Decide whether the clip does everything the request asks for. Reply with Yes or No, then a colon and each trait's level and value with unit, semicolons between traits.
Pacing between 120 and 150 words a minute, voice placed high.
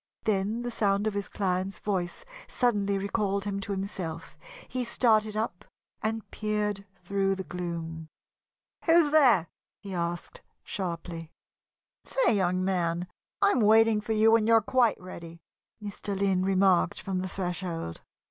Yes: average, 140 wpm; high, 195 Hz